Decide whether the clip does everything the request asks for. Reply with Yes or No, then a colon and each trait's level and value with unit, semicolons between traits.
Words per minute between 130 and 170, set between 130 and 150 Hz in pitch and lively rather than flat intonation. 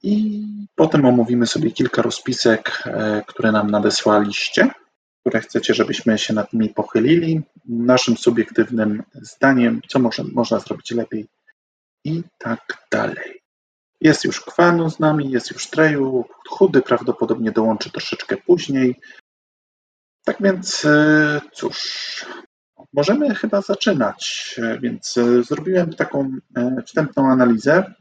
No: slow, 110 wpm; low, 135 Hz; wide, 6.9 semitones